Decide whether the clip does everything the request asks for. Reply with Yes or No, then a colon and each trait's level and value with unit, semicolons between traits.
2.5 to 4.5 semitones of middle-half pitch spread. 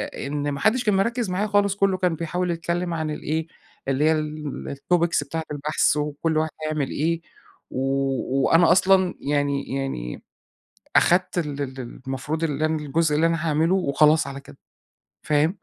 Yes: average, 3.2 semitones